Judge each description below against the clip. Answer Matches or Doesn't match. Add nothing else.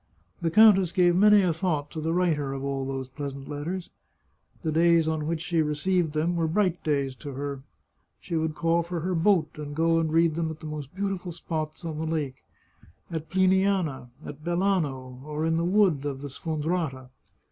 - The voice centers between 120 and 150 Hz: Doesn't match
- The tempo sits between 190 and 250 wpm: Matches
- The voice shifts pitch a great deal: Doesn't match